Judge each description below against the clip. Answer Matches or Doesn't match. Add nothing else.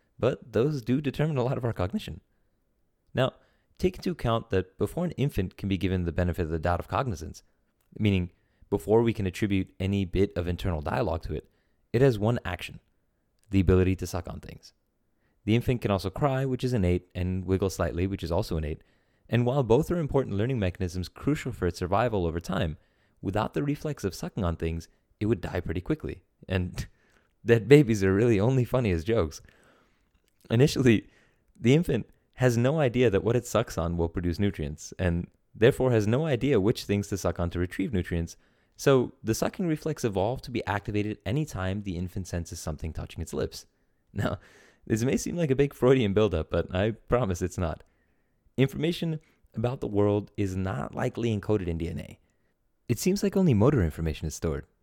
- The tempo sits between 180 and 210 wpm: Matches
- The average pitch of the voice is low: Matches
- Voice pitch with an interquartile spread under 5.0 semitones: Doesn't match